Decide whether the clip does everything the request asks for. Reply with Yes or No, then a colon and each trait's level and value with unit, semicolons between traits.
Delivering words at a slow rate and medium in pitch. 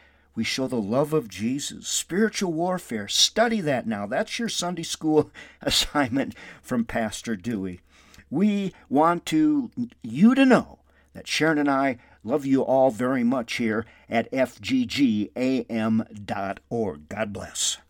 Yes: slow, 130 wpm; medium, 150 Hz